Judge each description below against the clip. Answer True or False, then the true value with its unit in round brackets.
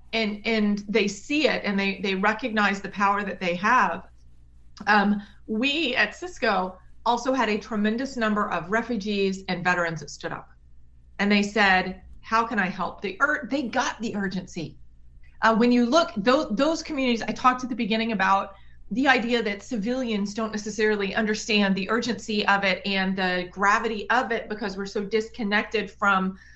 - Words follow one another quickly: False (175 wpm)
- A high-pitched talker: True (210 Hz)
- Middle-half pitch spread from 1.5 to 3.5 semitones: True (3.0 semitones)